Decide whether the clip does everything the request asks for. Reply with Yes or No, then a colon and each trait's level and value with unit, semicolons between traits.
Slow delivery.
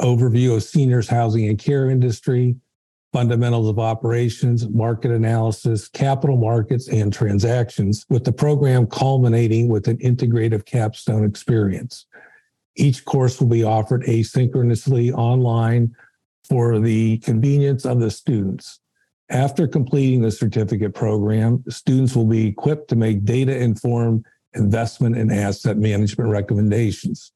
Yes: slow, 125 wpm